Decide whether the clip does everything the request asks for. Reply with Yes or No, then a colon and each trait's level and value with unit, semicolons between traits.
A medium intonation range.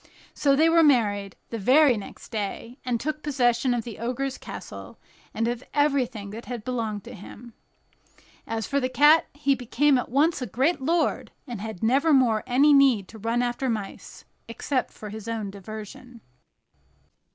Yes: average, 3.8 semitones